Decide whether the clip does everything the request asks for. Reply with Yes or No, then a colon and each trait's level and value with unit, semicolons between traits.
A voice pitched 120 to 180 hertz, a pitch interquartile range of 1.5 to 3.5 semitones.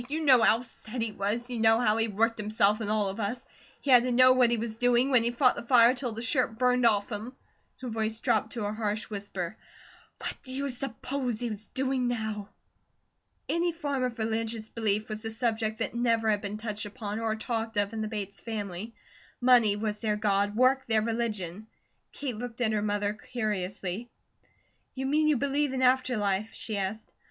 No: high, 225 Hz; average, 2.7 semitones